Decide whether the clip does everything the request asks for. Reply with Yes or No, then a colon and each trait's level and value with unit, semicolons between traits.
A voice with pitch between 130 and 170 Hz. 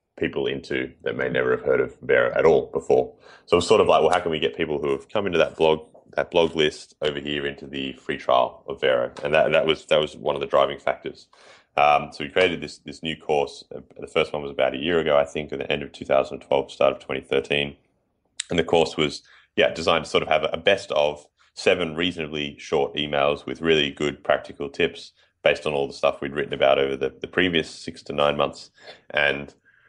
No: very low, 75 Hz